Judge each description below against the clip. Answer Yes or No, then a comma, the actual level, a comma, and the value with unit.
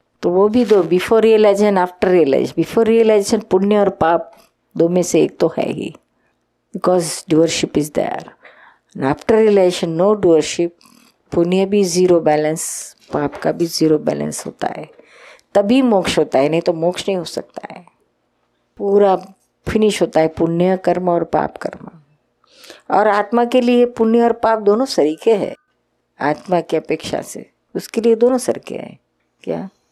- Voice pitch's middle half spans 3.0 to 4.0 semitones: No, average, 4.6 semitones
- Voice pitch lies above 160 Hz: Yes, high, 190 Hz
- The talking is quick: No, average, 160 wpm